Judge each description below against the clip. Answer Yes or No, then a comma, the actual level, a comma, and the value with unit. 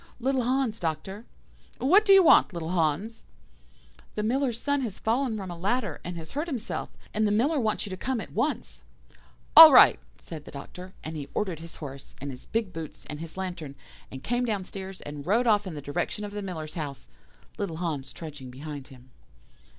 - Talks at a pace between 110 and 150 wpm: No, average, 195 wpm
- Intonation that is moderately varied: No, wide, 6.8 semitones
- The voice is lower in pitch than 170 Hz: No, high, 190 Hz